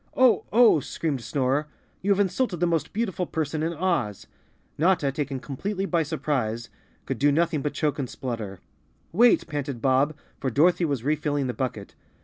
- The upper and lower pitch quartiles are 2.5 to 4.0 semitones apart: No, average, 4.7 semitones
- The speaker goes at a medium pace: Yes, average, 165 wpm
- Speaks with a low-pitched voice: No, medium, 150 Hz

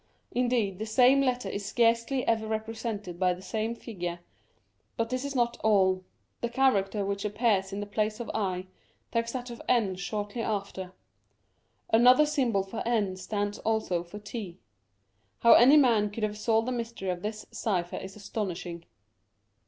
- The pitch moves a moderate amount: Yes, average, 3.4 semitones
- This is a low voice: No, high, 215 Hz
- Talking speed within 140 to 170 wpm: Yes, average, 160 wpm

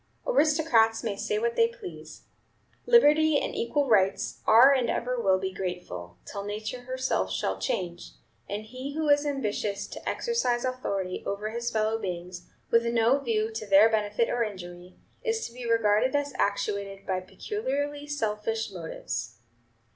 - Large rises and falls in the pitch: Yes, wide, 5.7 semitones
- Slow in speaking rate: No, average, 155 wpm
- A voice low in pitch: No, high, 225 Hz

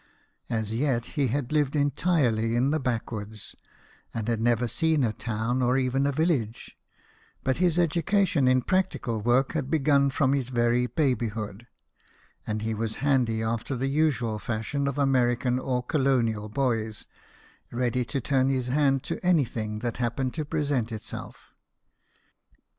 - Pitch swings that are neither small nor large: Yes, average, 3.6 semitones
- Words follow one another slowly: No, average, 145 wpm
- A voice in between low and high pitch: No, low, 125 Hz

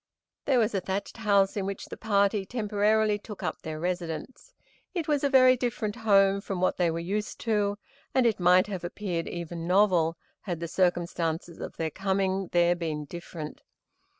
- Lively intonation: No, average, 3.4 semitones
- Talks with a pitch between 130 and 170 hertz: No, high, 195 Hz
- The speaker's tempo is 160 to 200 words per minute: Yes, average, 180 wpm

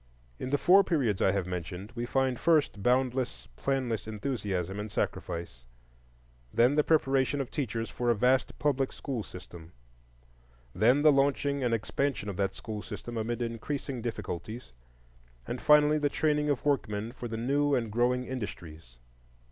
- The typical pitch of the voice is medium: No, low, 120 Hz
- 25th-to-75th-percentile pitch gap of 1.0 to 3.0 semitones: No, average, 4.9 semitones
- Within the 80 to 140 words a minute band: No, average, 155 wpm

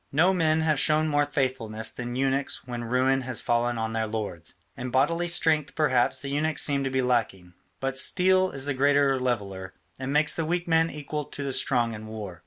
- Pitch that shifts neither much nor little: Yes, average, 4.2 semitones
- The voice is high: No, low, 135 Hz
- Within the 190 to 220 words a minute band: Yes, average, 200 wpm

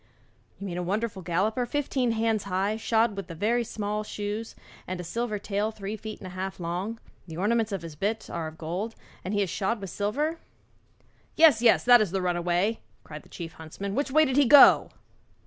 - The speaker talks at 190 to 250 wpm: Yes, average, 200 wpm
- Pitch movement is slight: No, average, 3.8 semitones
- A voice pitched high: Yes, high, 205 Hz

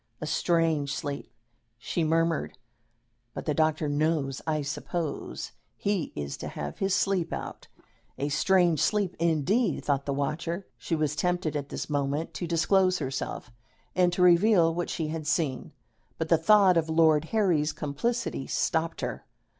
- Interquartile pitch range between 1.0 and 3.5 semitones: Yes, average, 3.2 semitones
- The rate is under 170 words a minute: Yes, average, 155 wpm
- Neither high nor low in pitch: Yes, medium, 160 Hz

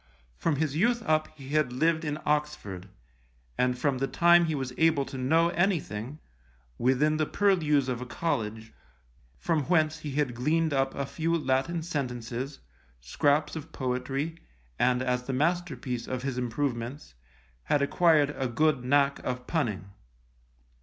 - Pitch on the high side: No, medium, 140 Hz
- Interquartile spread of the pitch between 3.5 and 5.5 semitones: Yes, average, 3.8 semitones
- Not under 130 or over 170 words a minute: Yes, average, 150 wpm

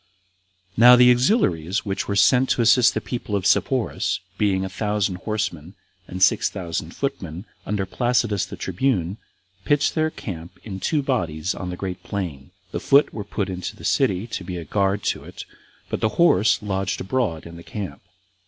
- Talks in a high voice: No, low, 100 Hz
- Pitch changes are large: No, average, 4.6 semitones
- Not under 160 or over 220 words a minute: Yes, average, 180 wpm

